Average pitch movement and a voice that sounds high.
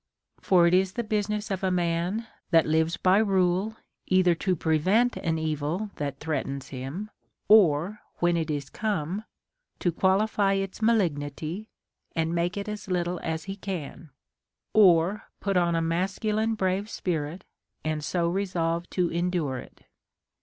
No: average, 3.6 semitones; medium, 180 Hz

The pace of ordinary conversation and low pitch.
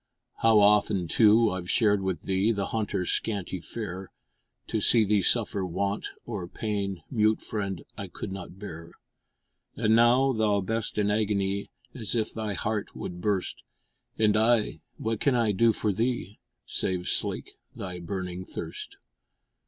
Yes: average, 150 wpm; low, 105 Hz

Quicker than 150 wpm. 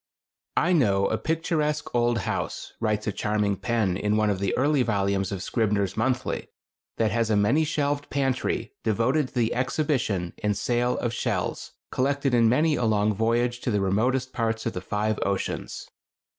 Yes: average, 175 wpm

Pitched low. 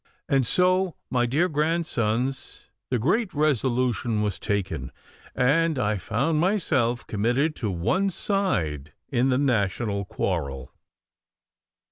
Yes: low, 125 Hz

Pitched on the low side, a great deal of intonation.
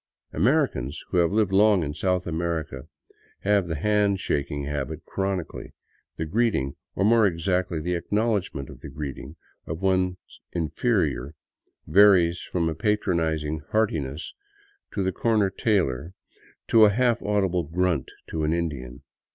No: very low, 90 Hz; average, 4.7 semitones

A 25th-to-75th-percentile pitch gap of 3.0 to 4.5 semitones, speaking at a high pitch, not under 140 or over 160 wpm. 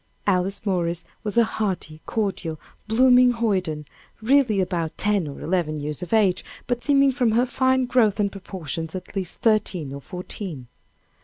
No: wide, 5.5 semitones; high, 195 Hz; average, 155 wpm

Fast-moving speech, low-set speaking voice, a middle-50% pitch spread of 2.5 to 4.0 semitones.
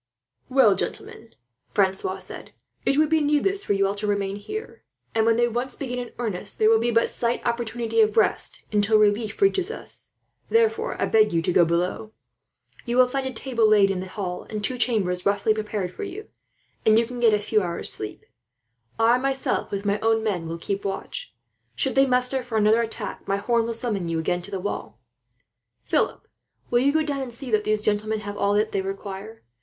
No: fast, 210 wpm; high, 220 Hz; average, 3.6 semitones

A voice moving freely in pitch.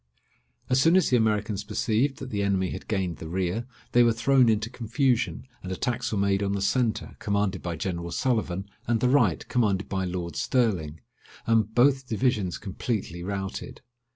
No: average, 4.3 semitones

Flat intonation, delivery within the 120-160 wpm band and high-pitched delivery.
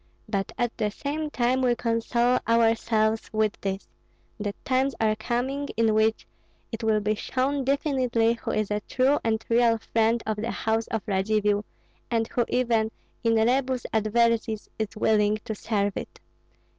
Yes: narrow, 2.1 semitones; average, 155 wpm; high, 225 Hz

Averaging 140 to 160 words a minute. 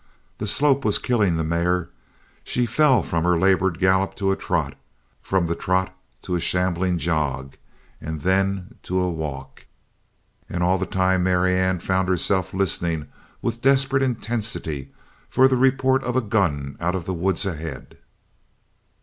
Yes: average, 155 wpm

